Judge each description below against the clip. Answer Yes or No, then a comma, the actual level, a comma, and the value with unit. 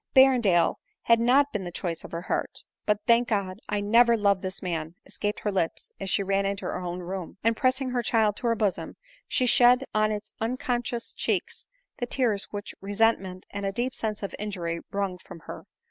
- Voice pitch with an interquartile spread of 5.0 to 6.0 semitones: No, average, 3.6 semitones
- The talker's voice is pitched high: Yes, high, 210 Hz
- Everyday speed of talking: No, fast, 210 wpm